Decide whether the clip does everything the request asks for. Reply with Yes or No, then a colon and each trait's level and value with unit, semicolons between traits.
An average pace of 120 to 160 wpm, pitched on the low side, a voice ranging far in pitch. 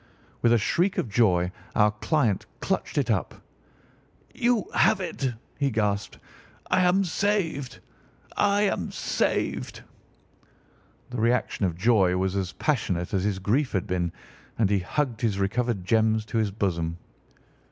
Yes: average, 140 wpm; low, 110 Hz; wide, 6.2 semitones